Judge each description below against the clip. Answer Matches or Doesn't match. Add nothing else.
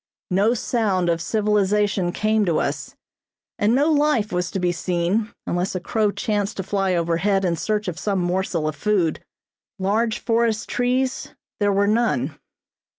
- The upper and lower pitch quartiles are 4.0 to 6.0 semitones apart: Doesn't match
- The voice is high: Matches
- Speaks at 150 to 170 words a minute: Matches